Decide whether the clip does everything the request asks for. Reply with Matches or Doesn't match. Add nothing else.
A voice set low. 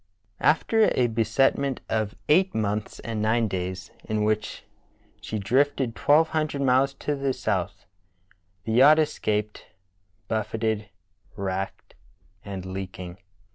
Matches